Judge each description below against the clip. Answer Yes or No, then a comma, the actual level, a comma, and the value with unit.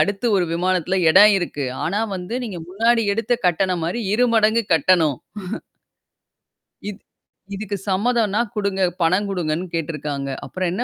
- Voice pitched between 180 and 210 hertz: Yes, high, 190 Hz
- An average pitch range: Yes, average, 3.7 semitones